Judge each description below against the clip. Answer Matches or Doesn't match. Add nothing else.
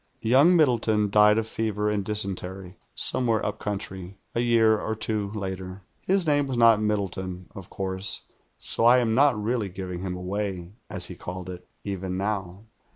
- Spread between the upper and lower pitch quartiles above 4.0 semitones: Doesn't match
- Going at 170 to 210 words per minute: Doesn't match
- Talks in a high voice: Doesn't match